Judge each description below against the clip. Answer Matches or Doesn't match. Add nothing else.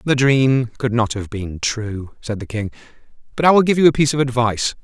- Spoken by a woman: Doesn't match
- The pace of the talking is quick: Matches